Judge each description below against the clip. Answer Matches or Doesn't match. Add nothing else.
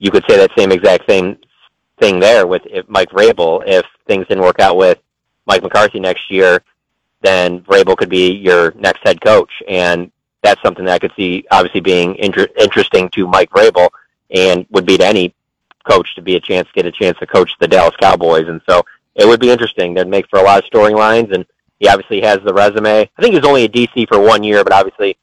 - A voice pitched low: Matches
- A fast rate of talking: Matches